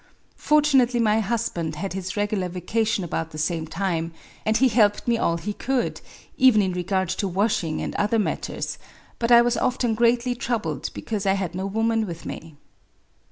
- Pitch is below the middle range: No, high, 205 Hz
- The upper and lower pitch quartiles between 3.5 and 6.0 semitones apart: Yes, average, 4.6 semitones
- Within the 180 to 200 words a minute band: Yes, average, 185 wpm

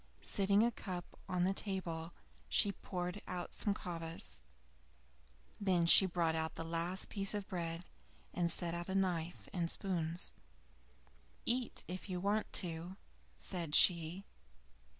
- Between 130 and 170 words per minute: Yes, slow, 135 wpm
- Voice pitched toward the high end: No, medium, 180 Hz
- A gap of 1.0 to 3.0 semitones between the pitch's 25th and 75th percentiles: Yes, narrow, 2.4 semitones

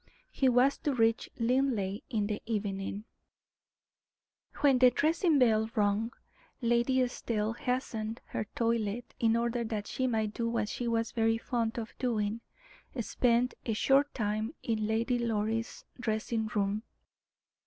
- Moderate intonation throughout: No, narrow, 2.2 semitones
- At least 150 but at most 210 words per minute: No, slow, 135 wpm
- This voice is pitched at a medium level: No, high, 230 Hz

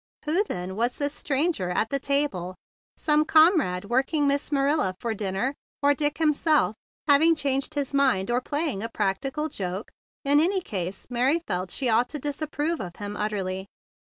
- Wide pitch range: Yes, wide, 6.7 semitones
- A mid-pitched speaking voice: No, very high, 275 Hz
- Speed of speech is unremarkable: Yes, average, 170 wpm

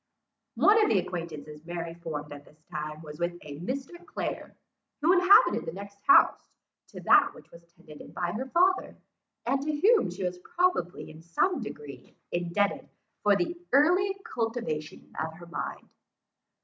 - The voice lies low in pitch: No, medium, 180 Hz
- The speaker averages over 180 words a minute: No, average, 160 wpm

